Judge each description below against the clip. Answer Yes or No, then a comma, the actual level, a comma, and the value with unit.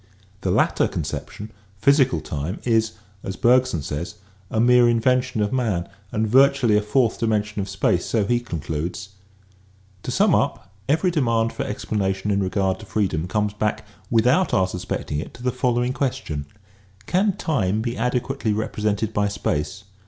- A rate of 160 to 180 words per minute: Yes, average, 165 wpm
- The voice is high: No, low, 110 Hz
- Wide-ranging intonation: No, average, 4.3 semitones